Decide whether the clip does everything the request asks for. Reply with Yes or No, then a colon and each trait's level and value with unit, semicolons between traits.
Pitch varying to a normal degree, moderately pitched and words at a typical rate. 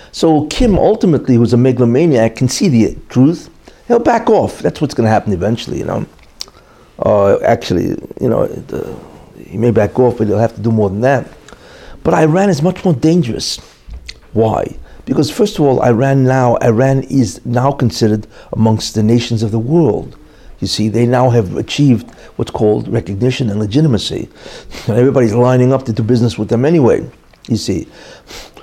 No: average, 3.6 semitones; low, 120 Hz; average, 175 wpm